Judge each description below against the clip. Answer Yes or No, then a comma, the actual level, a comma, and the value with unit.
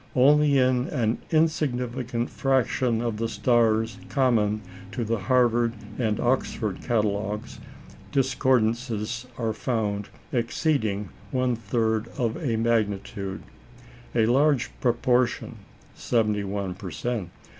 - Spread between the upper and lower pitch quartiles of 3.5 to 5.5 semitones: No, average, 2.9 semitones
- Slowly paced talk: Yes, slow, 100 wpm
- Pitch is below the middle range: Yes, low, 115 Hz